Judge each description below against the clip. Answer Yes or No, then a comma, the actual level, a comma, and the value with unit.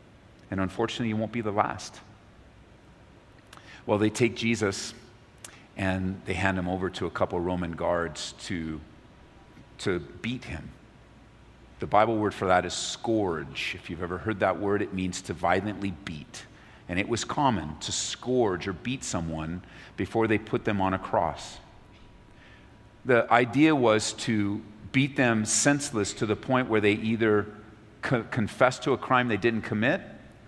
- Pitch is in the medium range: No, low, 105 Hz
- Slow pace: No, average, 160 wpm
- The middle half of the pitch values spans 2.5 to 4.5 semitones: Yes, average, 3.6 semitones